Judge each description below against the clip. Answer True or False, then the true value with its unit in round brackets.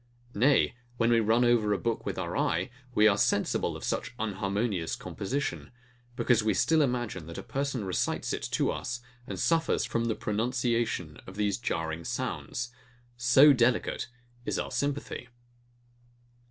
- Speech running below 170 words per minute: True (155 wpm)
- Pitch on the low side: True (115 Hz)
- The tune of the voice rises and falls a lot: False (3.6 semitones)